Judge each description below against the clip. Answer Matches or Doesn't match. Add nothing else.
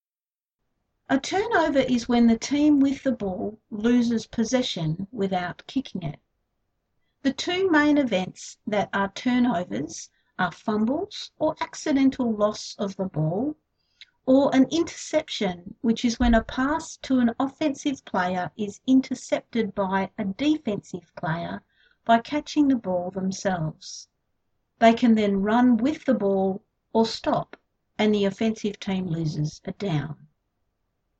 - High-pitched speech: Matches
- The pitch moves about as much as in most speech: Doesn't match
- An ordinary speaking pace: Doesn't match